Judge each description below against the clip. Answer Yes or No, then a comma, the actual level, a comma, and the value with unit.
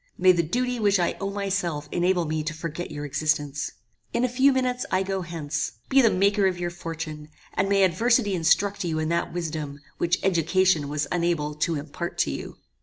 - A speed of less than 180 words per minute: No, average, 195 wpm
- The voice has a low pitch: No, medium, 175 Hz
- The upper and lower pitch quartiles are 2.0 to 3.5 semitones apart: No, average, 4.1 semitones